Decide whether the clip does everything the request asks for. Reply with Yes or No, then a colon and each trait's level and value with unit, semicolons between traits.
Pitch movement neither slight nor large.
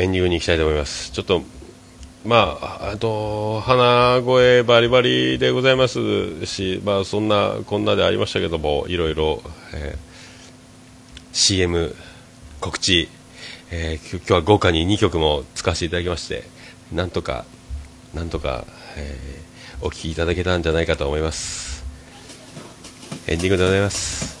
Yes: average, 4.8 semitones